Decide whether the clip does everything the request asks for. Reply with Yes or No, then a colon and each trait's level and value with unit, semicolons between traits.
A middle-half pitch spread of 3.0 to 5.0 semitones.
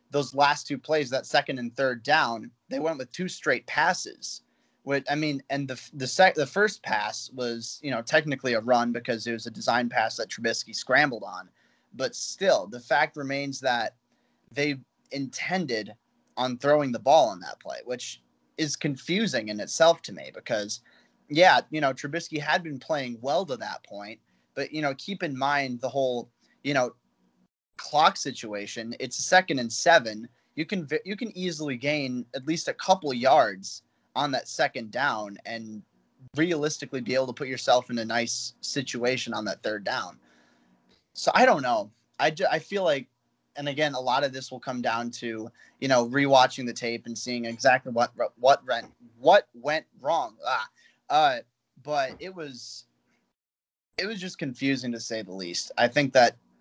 Yes: average, 4.2 semitones